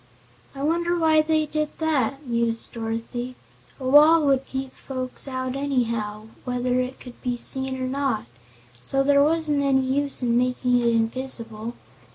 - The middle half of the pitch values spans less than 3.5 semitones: Yes, average, 2.8 semitones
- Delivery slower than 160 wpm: Yes, average, 150 wpm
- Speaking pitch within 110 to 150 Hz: No, very high, 260 Hz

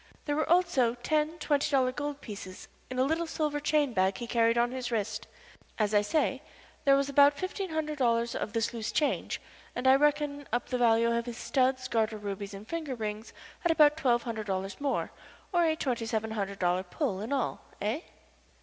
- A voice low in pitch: No, very high, 250 Hz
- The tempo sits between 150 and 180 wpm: No, average, 200 wpm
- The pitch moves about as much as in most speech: Yes, average, 4.8 semitones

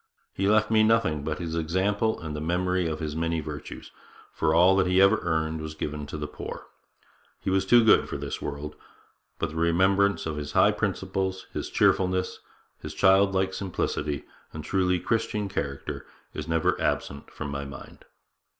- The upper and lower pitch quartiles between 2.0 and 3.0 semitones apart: No, average, 3.8 semitones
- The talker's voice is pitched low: Yes, very low, 85 Hz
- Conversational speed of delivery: Yes, average, 175 wpm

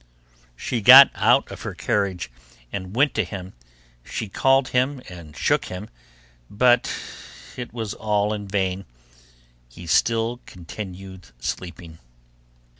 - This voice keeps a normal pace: No, slow, 120 wpm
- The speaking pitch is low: Yes, low, 100 Hz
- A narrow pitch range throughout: No, average, 4.6 semitones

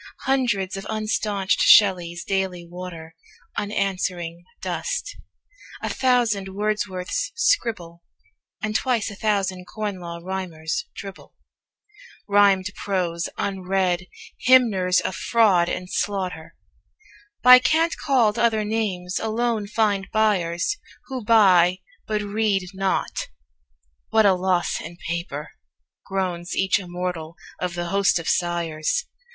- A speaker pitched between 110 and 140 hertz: No, high, 195 Hz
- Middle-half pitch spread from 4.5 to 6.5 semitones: No, average, 3.3 semitones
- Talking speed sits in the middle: No, slow, 110 wpm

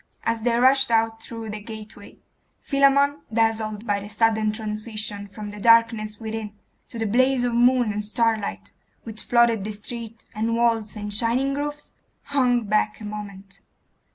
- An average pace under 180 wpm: Yes, average, 155 wpm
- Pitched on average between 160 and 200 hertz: No, high, 225 Hz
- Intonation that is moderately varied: No, narrow, 2.0 semitones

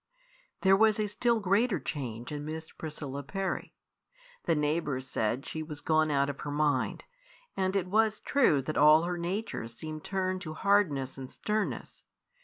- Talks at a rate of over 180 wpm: No, average, 165 wpm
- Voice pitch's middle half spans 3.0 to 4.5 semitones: No, average, 5.1 semitones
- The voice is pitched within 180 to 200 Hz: No, medium, 155 Hz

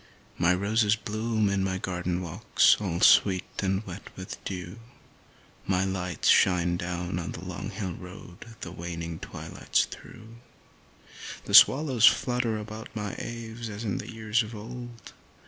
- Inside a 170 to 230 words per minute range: No, average, 150 wpm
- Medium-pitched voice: No, low, 100 Hz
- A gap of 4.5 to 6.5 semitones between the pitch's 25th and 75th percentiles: No, average, 3.7 semitones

